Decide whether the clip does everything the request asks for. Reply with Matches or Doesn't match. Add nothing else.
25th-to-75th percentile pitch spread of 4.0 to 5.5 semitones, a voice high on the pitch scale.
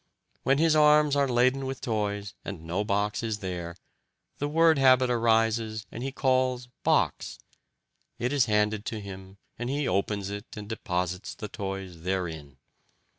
Doesn't match